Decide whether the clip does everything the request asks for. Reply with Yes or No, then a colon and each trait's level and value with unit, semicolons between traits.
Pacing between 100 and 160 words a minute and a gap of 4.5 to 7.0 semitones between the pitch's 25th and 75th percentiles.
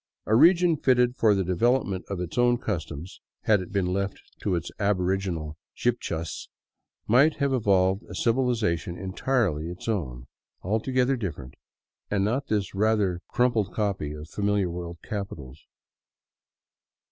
Yes: average, 140 wpm; average, 5.2 semitones